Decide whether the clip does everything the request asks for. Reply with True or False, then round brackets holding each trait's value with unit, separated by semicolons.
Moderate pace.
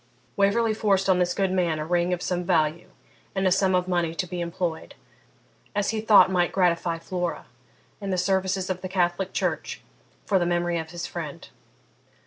True (185 wpm)